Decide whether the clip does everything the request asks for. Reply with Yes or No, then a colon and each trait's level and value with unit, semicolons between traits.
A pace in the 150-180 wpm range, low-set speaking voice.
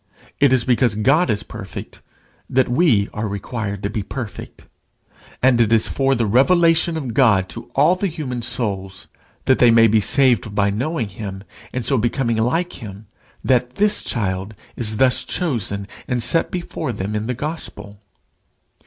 Yes: average, 165 wpm; low, 120 Hz